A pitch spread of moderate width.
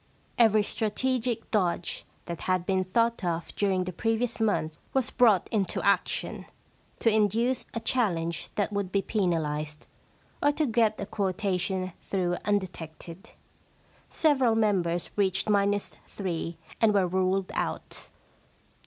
Yes: average, 3.6 semitones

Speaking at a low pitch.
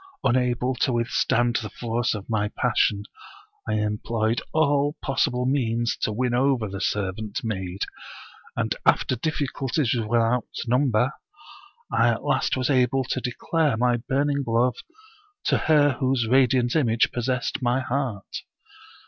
Yes: low, 125 Hz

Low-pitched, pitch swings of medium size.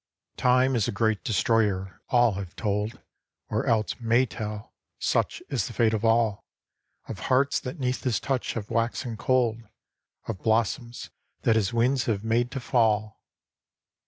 No: low, 115 Hz; narrow, 2.3 semitones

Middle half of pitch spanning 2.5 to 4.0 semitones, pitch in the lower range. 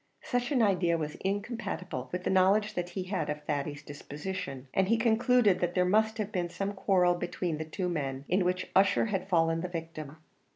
No: average, 3.5 semitones; medium, 180 Hz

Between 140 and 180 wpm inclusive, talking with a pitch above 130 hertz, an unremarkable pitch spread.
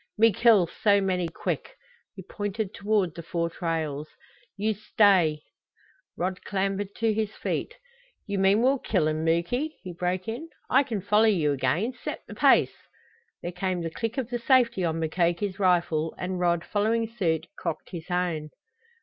Yes: average, 165 wpm; high, 190 Hz; average, 4.3 semitones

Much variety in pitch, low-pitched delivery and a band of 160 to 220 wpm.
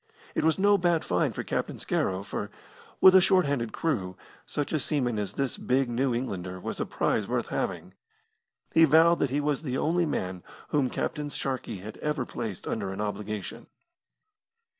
Yes: wide, 6.9 semitones; low, 130 Hz; average, 180 wpm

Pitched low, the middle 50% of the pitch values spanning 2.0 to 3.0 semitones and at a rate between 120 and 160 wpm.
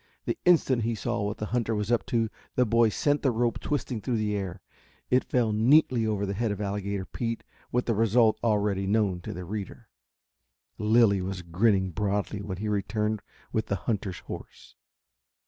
No: low, 105 Hz; narrow, 2.6 semitones; average, 180 wpm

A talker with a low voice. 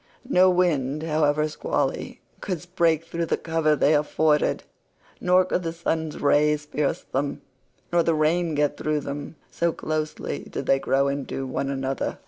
No: medium, 155 Hz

